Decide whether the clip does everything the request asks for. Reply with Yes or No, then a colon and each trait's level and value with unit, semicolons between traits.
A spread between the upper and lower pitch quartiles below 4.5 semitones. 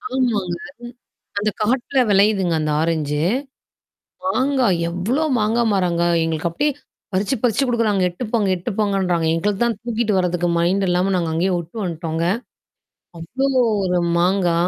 No: average, 4.8 semitones